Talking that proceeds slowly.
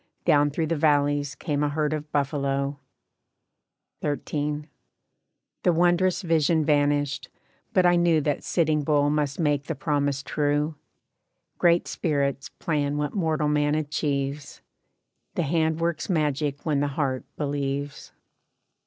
Yes: slow, 125 wpm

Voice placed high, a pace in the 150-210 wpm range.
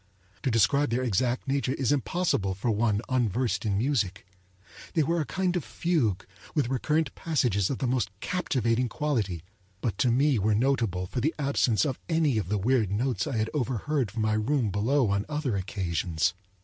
No: low, 120 Hz; average, 180 wpm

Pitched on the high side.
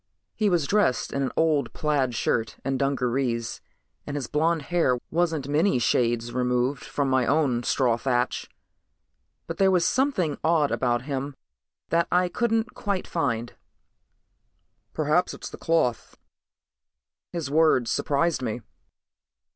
No: medium, 145 Hz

